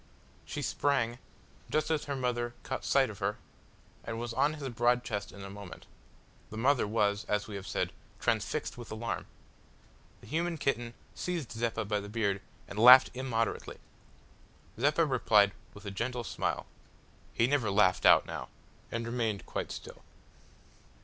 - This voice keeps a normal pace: Yes, average, 155 wpm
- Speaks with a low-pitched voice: Yes, low, 115 Hz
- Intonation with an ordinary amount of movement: Yes, average, 3.9 semitones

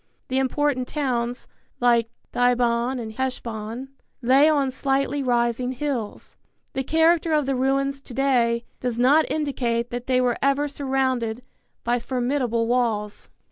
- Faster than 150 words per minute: No, slow, 135 wpm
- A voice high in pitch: Yes, very high, 255 Hz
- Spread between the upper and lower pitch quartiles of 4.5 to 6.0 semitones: No, narrow, 2.5 semitones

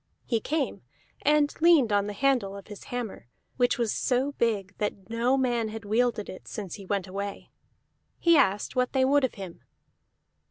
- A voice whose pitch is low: No, high, 230 Hz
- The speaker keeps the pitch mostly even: No, average, 4.6 semitones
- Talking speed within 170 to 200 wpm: Yes, average, 175 wpm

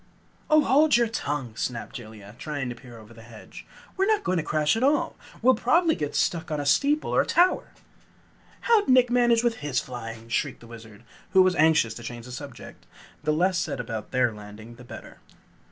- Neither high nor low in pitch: Yes, medium, 145 Hz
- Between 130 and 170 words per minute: No, average, 200 wpm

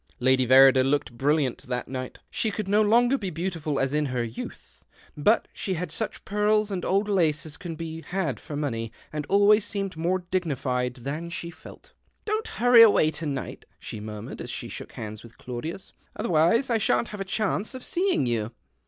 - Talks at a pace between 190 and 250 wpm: Yes, fast, 205 wpm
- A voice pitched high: No, medium, 160 Hz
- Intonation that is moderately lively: No, wide, 7.4 semitones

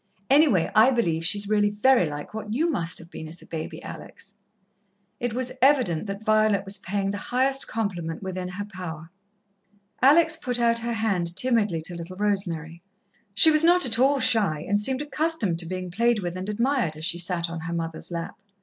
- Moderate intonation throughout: No, wide, 6.1 semitones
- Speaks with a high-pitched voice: Yes, high, 205 Hz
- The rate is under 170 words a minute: No, average, 195 wpm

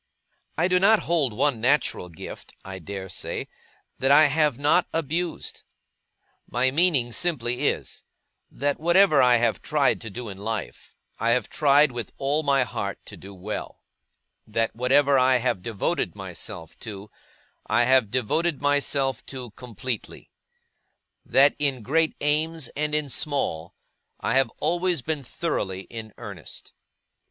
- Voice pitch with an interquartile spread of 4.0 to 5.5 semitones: Yes, average, 4.8 semitones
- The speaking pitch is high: No, low, 135 Hz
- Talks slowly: No, average, 145 wpm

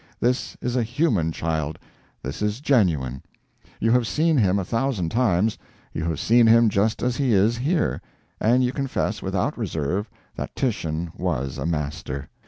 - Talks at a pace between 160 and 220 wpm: Yes, average, 165 wpm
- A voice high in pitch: No, low, 105 Hz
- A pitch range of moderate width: No, wide, 7.0 semitones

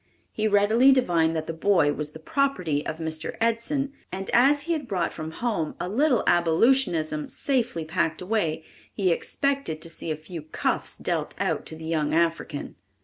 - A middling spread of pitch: No, wide, 7.0 semitones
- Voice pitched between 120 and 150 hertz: No, medium, 175 Hz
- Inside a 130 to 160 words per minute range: No, average, 175 wpm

